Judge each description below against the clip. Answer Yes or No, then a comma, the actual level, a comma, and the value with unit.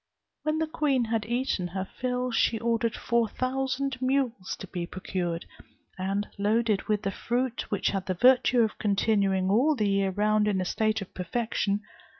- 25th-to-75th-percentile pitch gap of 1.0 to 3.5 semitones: No, average, 4.2 semitones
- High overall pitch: Yes, high, 215 Hz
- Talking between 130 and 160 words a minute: No, average, 170 wpm